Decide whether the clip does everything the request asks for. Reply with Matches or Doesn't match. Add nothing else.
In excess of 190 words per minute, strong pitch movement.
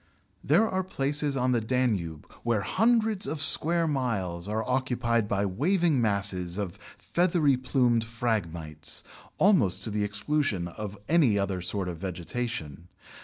Doesn't match